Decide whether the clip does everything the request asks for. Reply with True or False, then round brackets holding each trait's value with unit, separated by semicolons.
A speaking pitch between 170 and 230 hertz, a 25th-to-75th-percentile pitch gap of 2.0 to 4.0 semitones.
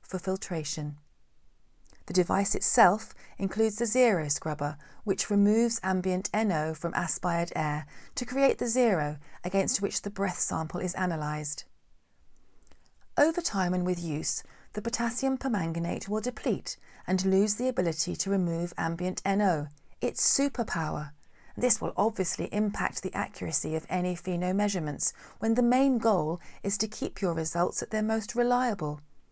False (190 Hz; 4.8 semitones)